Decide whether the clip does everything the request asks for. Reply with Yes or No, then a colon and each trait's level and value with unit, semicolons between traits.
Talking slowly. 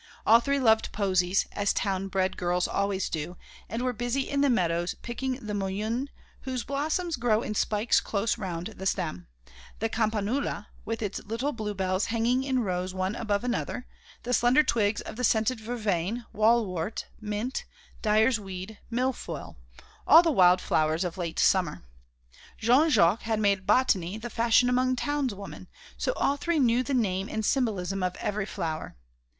No: average, 165 wpm